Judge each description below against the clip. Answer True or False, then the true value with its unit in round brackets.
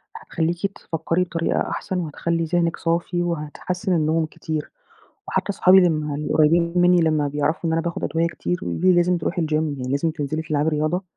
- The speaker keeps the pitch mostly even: True (2.1 semitones)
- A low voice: False (165 Hz)